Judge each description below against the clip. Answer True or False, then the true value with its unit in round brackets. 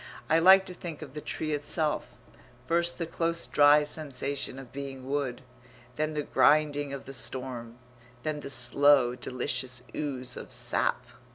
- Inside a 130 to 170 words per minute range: True (155 wpm)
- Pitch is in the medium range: True (145 Hz)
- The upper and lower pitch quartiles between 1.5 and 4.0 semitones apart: True (2.9 semitones)